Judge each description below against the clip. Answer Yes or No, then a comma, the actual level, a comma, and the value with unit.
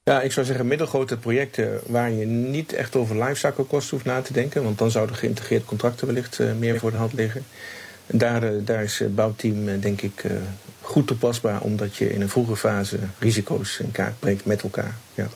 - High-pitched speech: No, low, 115 Hz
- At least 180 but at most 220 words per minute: Yes, average, 195 wpm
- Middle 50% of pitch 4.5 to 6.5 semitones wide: No, average, 3.4 semitones